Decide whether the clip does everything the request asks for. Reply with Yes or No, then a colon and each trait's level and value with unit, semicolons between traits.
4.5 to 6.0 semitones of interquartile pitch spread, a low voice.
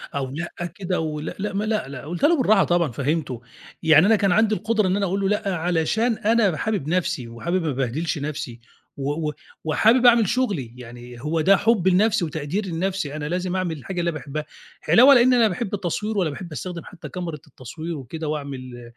No: average, 5.3 semitones; medium, 175 Hz